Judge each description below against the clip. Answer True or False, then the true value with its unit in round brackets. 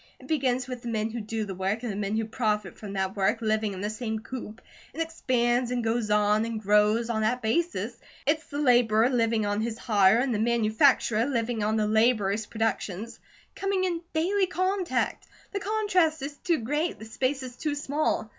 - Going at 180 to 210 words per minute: True (200 wpm)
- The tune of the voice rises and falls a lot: False (4.4 semitones)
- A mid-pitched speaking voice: False (230 Hz)